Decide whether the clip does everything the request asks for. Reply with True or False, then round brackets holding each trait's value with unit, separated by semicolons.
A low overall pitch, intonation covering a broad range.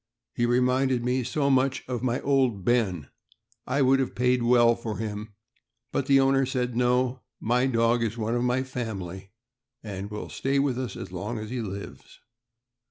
False (125 Hz; 2.7 semitones)